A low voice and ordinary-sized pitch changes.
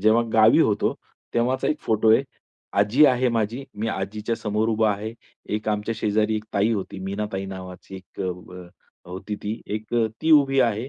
No: low, 110 Hz; narrow, 2.3 semitones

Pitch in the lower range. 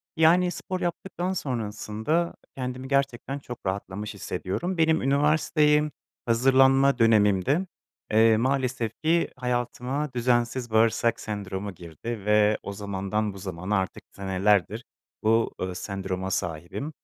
Yes: low, 115 Hz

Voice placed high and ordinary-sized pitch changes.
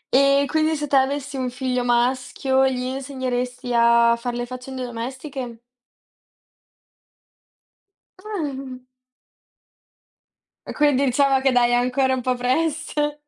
No: very high, 260 Hz; narrow, 1.9 semitones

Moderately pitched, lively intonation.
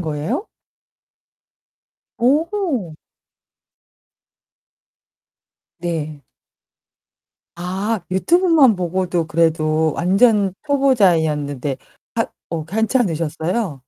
Yes: medium, 180 Hz; wide, 6.9 semitones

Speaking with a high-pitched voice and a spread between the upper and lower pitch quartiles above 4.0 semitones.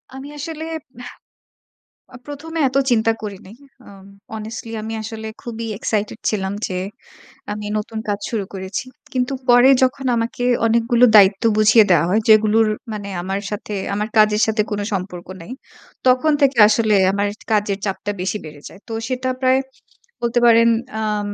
No: high, 220 Hz; average, 2.9 semitones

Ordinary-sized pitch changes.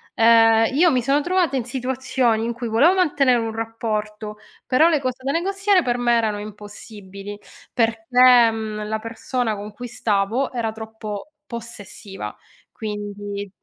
Yes: average, 3.2 semitones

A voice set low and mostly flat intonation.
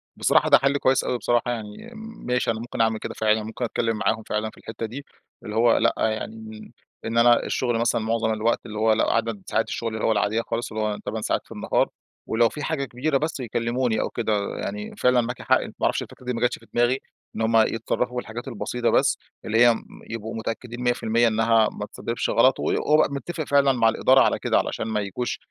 Yes: low, 115 Hz; narrow, 2.2 semitones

